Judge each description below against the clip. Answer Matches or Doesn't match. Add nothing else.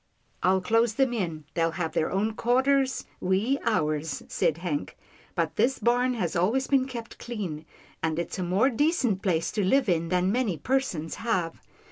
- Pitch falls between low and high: Doesn't match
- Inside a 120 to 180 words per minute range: Doesn't match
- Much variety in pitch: Matches